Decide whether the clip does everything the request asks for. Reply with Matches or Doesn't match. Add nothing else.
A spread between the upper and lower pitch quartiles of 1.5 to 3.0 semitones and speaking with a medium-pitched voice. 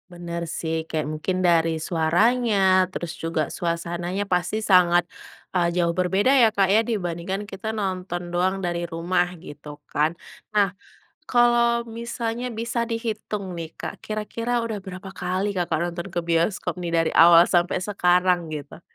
Doesn't match